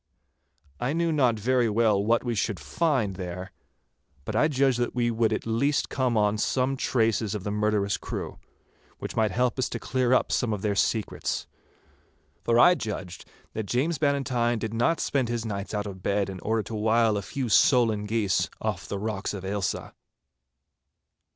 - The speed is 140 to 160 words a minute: No, average, 180 wpm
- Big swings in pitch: No, average, 3.3 semitones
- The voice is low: Yes, low, 110 Hz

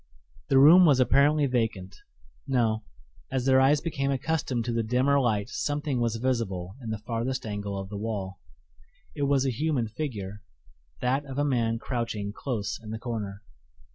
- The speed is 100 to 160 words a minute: No, average, 170 wpm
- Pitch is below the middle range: Yes, low, 120 Hz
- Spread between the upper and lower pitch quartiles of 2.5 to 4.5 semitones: Yes, average, 4.1 semitones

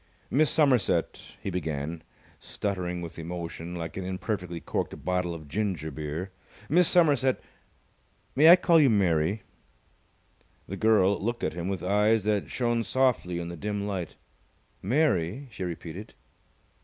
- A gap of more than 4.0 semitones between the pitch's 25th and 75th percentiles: Yes, average, 5.0 semitones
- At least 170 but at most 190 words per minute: No, average, 145 wpm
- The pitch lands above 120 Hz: No, very low, 95 Hz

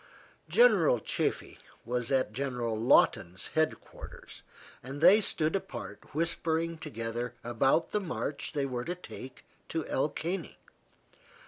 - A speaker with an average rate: No, slow, 125 wpm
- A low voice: No, medium, 145 Hz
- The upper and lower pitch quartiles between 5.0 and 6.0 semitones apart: Yes, average, 5.3 semitones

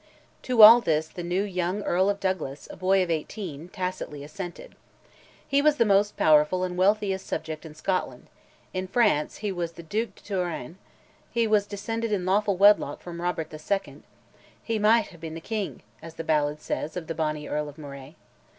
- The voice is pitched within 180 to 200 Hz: Yes, medium, 185 Hz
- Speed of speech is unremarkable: Yes, average, 185 wpm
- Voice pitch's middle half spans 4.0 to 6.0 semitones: Yes, average, 4.3 semitones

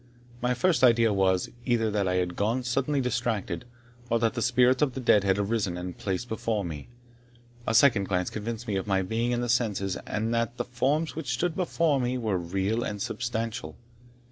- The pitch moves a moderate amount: Yes, average, 3.8 semitones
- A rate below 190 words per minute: No, average, 200 wpm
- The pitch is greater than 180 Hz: No, low, 115 Hz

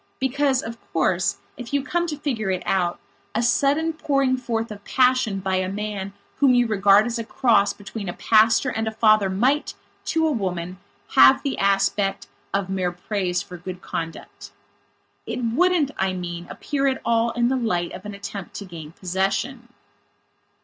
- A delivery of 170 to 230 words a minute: Yes, average, 175 wpm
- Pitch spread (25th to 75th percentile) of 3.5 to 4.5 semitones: No, average, 5.1 semitones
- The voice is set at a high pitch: Yes, high, 215 Hz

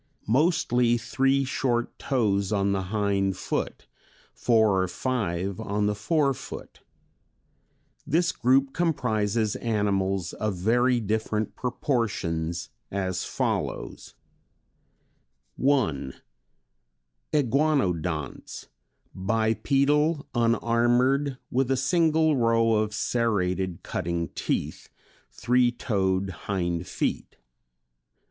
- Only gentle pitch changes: No, average, 5.0 semitones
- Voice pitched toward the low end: Yes, low, 110 Hz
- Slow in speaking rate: Yes, slow, 85 wpm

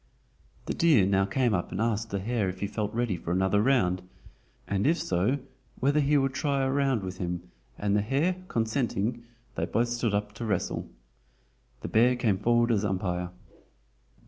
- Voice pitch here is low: Yes, low, 110 Hz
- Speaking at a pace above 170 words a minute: Yes, average, 180 wpm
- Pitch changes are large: No, average, 4.6 semitones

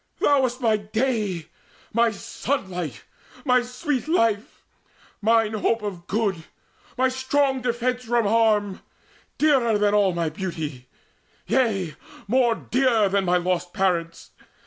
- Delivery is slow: Yes, slow, 125 wpm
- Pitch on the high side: Yes, high, 220 Hz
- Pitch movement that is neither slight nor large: Yes, average, 4.8 semitones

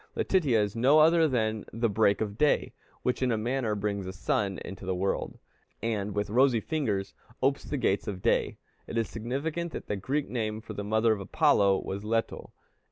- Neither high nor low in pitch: No, low, 110 Hz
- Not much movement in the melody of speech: No, average, 4.3 semitones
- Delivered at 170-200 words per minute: Yes, average, 195 wpm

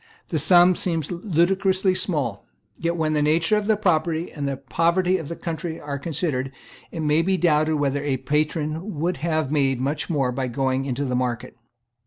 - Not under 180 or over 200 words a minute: Yes, average, 185 wpm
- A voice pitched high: No, medium, 155 Hz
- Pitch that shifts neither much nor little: Yes, average, 3.6 semitones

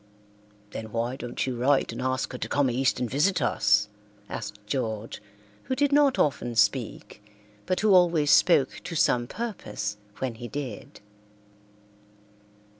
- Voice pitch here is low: Yes, low, 130 Hz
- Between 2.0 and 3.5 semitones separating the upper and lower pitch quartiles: No, wide, 5.4 semitones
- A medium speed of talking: Yes, average, 145 wpm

